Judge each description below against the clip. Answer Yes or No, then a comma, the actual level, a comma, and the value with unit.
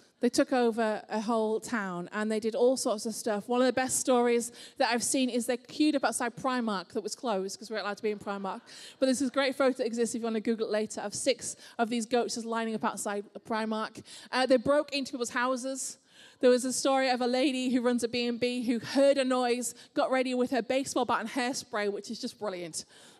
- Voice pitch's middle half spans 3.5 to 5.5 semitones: No, average, 2.7 semitones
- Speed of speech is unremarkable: No, fast, 250 wpm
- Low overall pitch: No, high, 240 Hz